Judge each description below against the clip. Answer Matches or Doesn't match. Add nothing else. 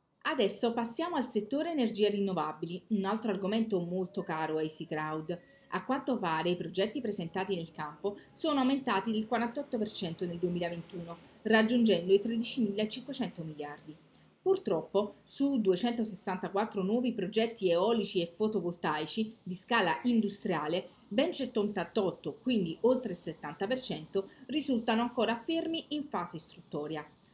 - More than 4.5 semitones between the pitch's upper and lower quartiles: Matches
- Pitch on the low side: Doesn't match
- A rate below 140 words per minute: Matches